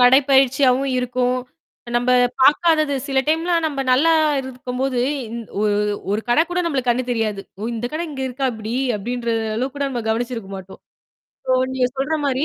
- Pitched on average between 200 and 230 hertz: No, very high, 255 Hz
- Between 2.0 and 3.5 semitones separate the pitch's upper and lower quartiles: Yes, narrow, 2.4 semitones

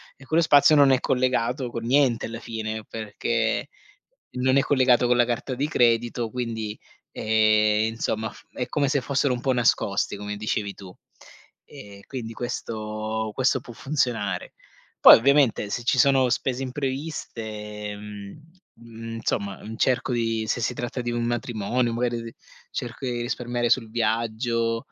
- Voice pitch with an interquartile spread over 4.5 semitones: No, narrow, 2.5 semitones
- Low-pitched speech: Yes, low, 115 Hz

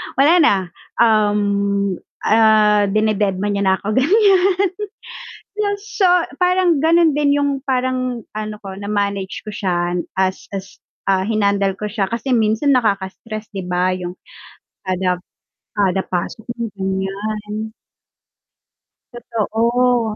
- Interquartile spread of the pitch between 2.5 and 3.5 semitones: No, average, 4.3 semitones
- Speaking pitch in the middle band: No, high, 215 Hz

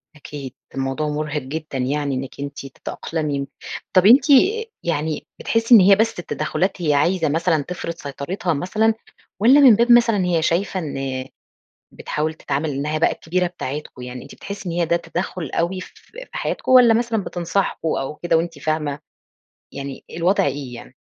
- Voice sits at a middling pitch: Yes, medium, 160 Hz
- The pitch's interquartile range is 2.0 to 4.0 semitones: No, average, 5.0 semitones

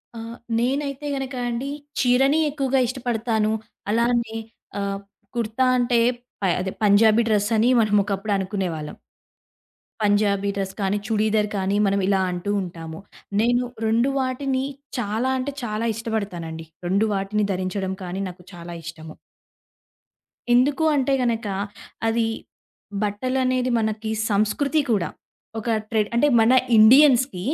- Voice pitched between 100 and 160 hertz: No, high, 220 Hz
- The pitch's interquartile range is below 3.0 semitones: No, average, 3.9 semitones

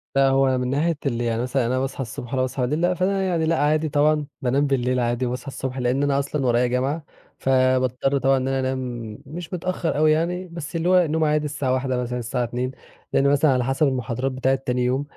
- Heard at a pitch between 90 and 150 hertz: Yes, low, 135 Hz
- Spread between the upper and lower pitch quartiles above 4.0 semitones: No, average, 3.2 semitones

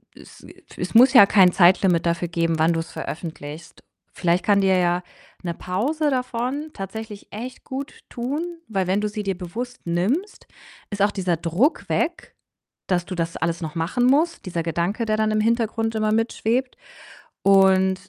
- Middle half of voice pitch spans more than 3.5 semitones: Yes, average, 5.3 semitones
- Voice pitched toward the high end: Yes, high, 200 Hz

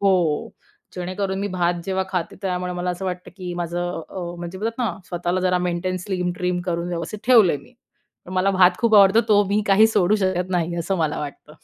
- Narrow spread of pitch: Yes, narrow, 1.7 semitones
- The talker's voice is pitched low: No, medium, 180 Hz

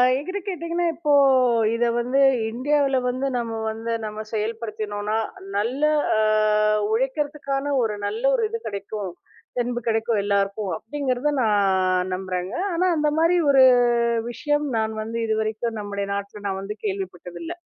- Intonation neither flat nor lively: No, wide, 5.9 semitones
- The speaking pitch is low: No, high, 225 Hz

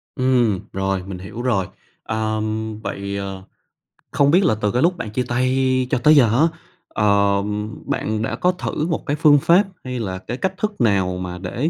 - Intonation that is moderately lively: No, wide, 5.8 semitones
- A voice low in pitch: Yes, low, 115 Hz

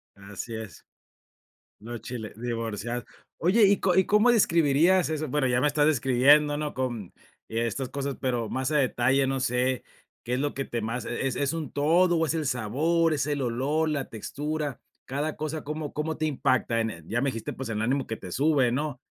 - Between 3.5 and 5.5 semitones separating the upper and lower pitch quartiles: Yes, average, 4.1 semitones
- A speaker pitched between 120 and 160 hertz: Yes, low, 135 Hz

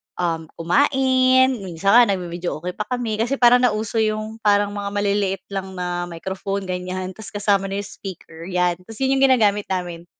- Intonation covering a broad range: No, average, 3.3 semitones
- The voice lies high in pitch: Yes, high, 200 Hz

